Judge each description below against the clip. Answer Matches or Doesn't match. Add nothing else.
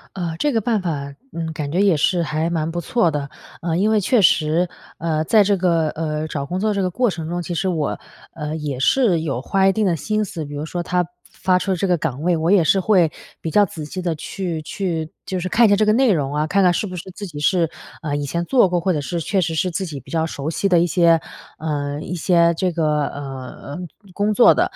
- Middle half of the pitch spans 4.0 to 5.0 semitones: Doesn't match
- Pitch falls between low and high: Matches